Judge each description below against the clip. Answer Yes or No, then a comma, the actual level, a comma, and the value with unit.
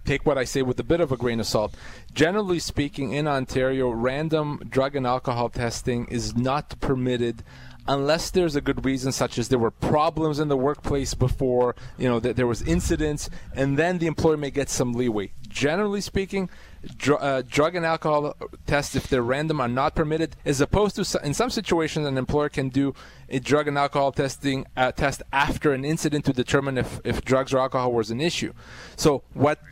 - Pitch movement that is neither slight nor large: Yes, average, 3.2 semitones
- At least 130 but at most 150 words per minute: No, average, 200 wpm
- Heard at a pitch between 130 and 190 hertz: Yes, medium, 140 Hz